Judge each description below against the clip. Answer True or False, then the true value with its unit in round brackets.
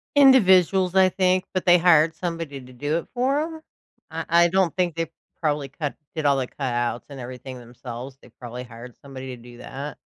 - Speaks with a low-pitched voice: False (150 Hz)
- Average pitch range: False (6.2 semitones)